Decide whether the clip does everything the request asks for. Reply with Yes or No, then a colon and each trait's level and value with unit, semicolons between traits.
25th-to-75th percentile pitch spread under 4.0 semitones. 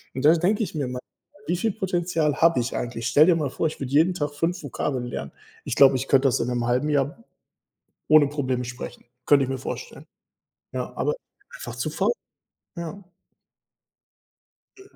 No: average, 4.8 semitones